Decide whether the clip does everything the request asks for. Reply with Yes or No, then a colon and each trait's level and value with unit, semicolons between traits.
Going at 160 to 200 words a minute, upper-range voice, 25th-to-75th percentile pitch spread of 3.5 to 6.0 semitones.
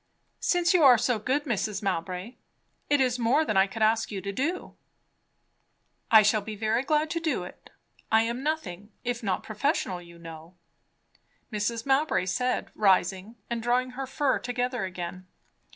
Yes: average, 170 wpm; high, 225 Hz; average, 5.2 semitones